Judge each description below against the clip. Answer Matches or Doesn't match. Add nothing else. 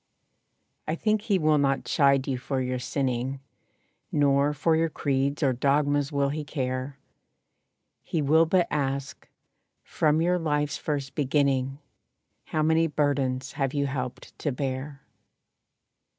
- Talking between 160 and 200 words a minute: Doesn't match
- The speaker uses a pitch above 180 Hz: Doesn't match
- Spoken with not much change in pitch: Matches